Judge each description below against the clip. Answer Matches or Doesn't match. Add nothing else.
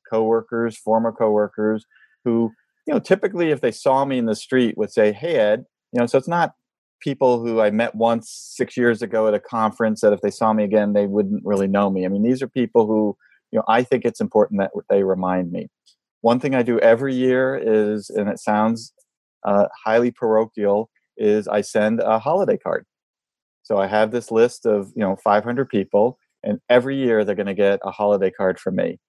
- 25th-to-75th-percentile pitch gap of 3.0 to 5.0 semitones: Doesn't match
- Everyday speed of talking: Doesn't match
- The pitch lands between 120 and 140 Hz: Doesn't match